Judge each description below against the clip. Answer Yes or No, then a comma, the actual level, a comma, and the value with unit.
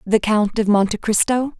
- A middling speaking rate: Yes, average, 190 wpm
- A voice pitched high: Yes, high, 215 Hz